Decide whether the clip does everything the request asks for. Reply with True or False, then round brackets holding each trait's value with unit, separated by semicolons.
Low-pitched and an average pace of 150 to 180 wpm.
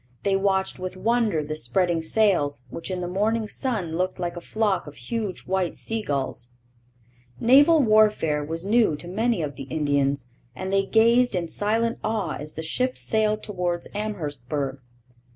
False (185 Hz; 165 wpm)